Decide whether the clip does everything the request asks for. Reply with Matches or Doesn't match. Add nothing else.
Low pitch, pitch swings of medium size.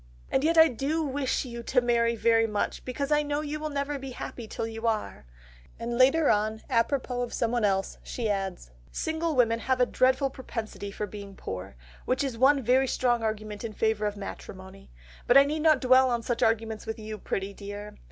Doesn't match